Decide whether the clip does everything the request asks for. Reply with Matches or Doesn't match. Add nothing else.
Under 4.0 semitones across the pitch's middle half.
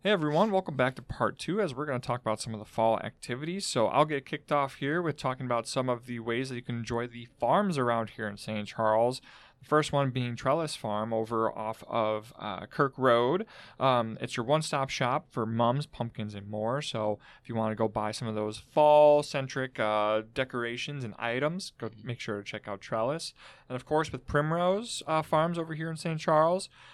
Doesn't match